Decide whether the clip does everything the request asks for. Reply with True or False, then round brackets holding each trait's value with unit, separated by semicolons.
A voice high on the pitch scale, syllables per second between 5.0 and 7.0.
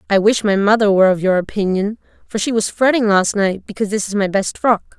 True (205 Hz; 6.0 syllables/s)